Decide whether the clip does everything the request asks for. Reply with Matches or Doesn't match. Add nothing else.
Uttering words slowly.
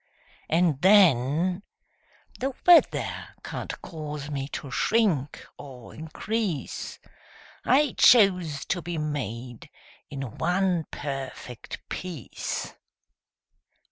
Matches